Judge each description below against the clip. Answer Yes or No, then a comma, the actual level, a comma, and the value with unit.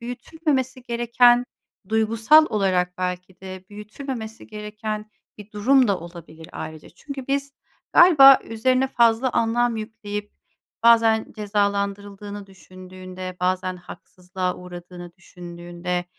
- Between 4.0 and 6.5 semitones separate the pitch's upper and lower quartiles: Yes, average, 4.5 semitones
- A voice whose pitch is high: Yes, high, 210 Hz